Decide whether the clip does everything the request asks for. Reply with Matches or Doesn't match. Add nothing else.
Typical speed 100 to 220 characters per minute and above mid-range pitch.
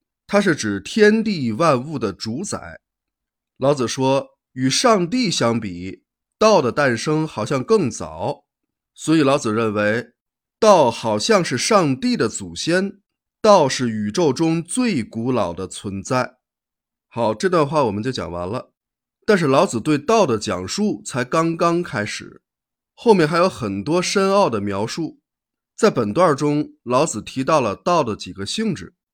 Doesn't match